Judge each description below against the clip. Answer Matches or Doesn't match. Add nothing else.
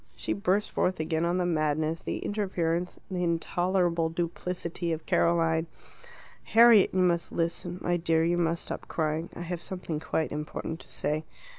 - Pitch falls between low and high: Matches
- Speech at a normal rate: Matches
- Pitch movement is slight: Matches